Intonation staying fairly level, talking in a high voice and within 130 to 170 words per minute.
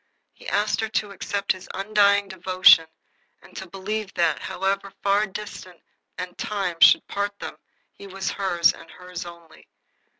Yes: narrow, 1.9 semitones; high, 195 Hz; average, 155 wpm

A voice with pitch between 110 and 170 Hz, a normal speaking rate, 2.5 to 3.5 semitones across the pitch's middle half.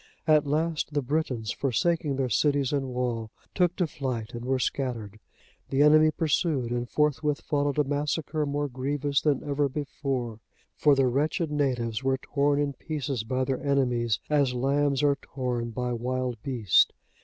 Yes: medium, 140 Hz; average, 160 wpm; average, 2.8 semitones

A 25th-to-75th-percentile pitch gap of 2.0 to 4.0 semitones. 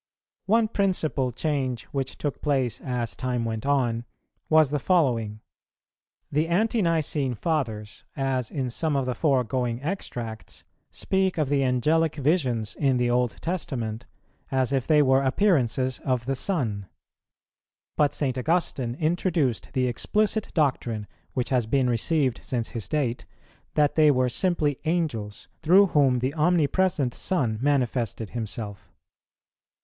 No: average, 4.4 semitones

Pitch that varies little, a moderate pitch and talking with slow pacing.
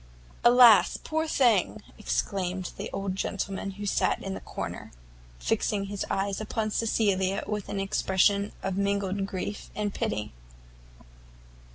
No: narrow, 1.6 semitones; high, 200 Hz; slow, 130 wpm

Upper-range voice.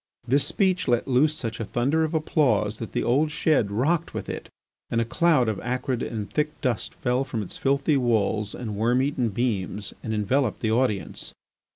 No: low, 125 Hz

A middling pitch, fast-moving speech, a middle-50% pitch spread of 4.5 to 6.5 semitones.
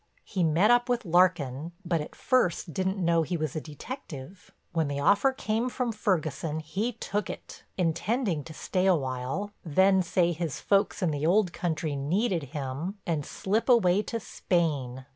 No: medium, 175 Hz; average, 170 wpm; average, 4.8 semitones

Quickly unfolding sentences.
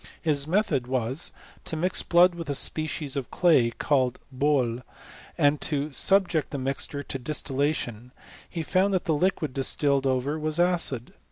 No: average, 155 wpm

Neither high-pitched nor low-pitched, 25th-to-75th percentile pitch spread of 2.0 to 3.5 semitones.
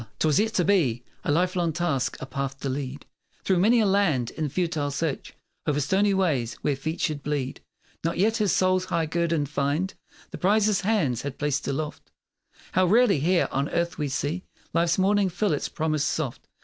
No: medium, 165 Hz; average, 4.8 semitones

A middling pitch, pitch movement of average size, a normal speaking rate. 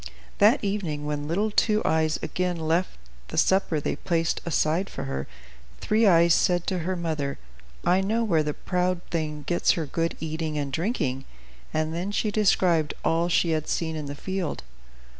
Yes: medium, 165 Hz; average, 3.1 semitones; average, 175 wpm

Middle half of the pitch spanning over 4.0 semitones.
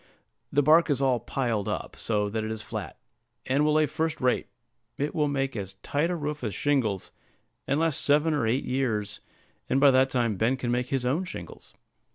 Yes: average, 4.5 semitones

